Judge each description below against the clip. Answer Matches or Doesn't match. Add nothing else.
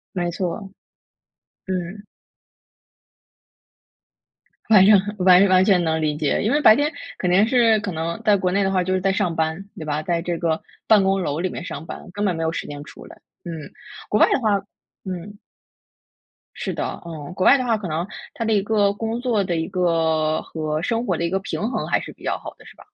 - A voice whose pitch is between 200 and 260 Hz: Doesn't match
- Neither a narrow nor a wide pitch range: Matches